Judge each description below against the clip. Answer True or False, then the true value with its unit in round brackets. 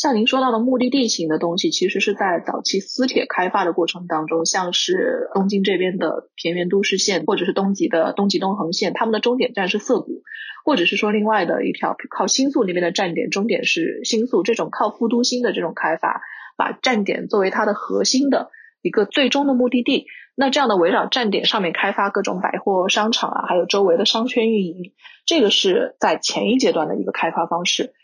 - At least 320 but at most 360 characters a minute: True (330 characters per minute)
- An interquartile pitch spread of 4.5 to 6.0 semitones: True (5.3 semitones)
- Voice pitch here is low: False (210 Hz)